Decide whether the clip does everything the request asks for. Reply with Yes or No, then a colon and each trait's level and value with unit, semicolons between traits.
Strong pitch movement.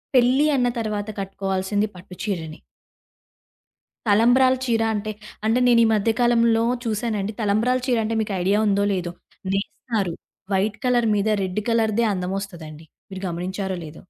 No: average, 3.3 semitones